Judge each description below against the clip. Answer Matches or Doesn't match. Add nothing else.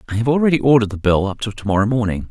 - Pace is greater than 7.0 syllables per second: Matches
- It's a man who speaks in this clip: Matches